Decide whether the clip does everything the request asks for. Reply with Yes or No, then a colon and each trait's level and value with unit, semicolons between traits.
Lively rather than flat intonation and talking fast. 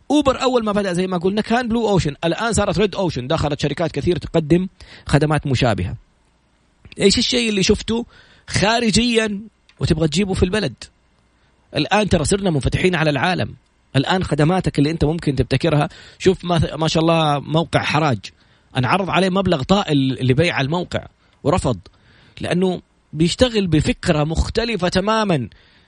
Yes: wide, 6.3 semitones; fast, 140 wpm